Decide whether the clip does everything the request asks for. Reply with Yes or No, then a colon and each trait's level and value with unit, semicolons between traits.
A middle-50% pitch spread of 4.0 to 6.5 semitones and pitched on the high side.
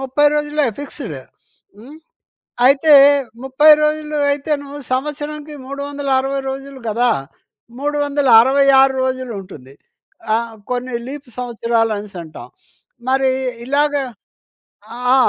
No: average, 2.9 semitones; very high, 270 Hz